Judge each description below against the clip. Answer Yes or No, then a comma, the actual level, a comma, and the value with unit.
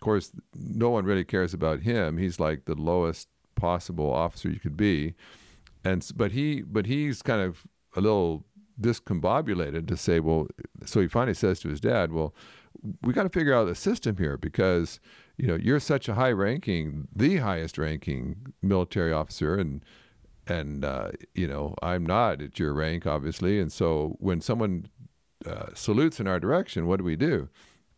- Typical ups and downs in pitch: Yes, average, 4.2 semitones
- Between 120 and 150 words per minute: No, average, 175 wpm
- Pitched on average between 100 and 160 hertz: No, very low, 90 Hz